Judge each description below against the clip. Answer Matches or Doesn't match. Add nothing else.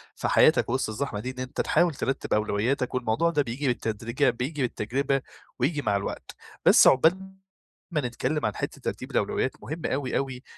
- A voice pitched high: Doesn't match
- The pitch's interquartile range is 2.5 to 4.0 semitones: Matches